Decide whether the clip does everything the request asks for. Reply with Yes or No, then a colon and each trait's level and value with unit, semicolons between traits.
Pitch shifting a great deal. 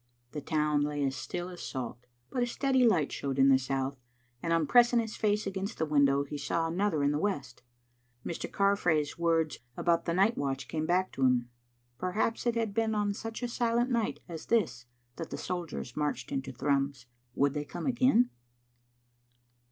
Yes: wide, 7.0 semitones